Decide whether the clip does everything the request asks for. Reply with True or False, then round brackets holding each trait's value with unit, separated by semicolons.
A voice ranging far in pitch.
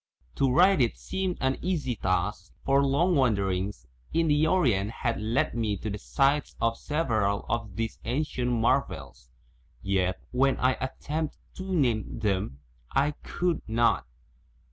True (6.0 semitones)